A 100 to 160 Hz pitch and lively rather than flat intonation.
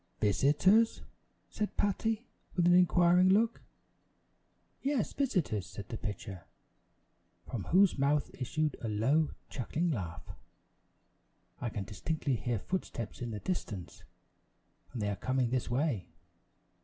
Yes: medium, 140 Hz; wide, 8.8 semitones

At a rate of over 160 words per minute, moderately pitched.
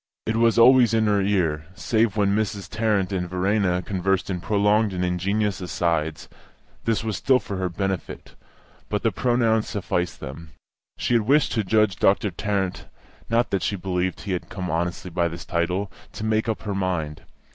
No: average, 180 wpm; low, 100 Hz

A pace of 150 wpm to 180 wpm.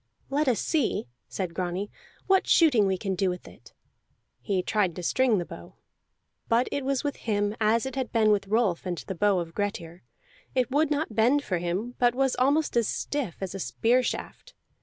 No: average, 200 wpm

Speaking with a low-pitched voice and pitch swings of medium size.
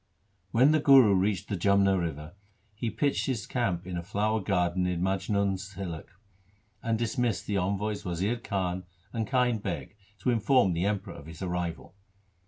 Yes: low, 100 Hz; average, 3.6 semitones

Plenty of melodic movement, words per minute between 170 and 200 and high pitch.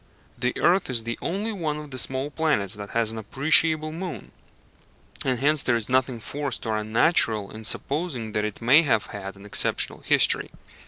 No: wide, 5.8 semitones; average, 180 wpm; low, 130 Hz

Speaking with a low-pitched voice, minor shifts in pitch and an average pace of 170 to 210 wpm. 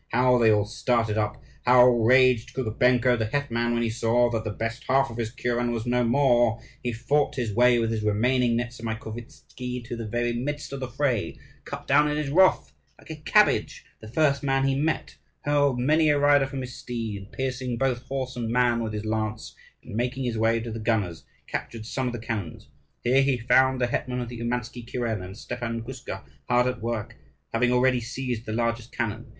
Yes: low, 120 Hz; narrow, 2.1 semitones; average, 200 wpm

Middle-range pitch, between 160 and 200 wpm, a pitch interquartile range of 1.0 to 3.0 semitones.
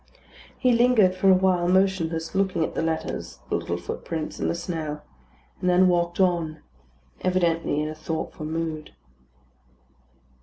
No: medium, 170 Hz; average, 140 wpm; average, 2.7 semitones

